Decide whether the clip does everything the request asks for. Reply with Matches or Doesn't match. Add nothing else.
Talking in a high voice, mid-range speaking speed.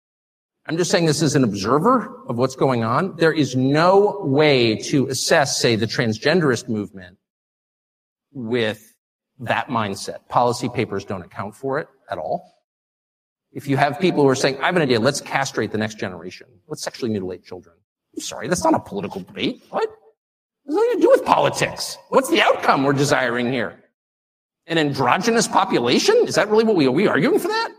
Doesn't match